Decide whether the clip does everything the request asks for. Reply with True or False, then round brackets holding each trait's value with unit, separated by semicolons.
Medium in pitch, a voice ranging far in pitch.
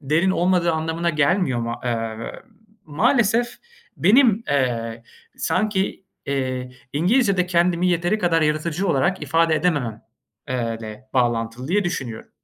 True (160 Hz; 6.2 semitones)